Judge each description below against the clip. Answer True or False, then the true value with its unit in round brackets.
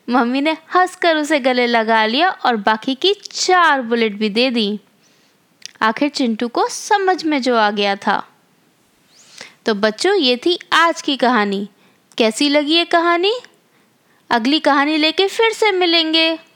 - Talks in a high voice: True (290 Hz)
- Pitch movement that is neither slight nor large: False (7.1 semitones)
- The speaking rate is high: False (150 wpm)